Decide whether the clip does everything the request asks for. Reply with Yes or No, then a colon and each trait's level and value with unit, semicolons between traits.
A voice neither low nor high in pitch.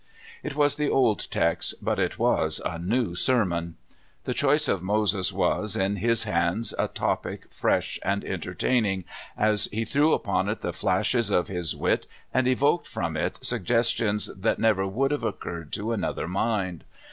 No: low, 105 Hz